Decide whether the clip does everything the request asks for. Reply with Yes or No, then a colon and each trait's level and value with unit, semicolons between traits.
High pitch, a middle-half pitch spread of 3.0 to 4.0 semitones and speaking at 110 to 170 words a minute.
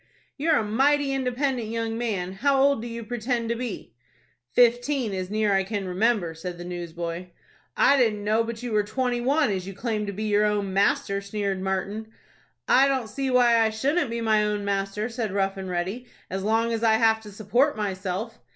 No: high, 220 Hz; average, 3.6 semitones; fast, 205 wpm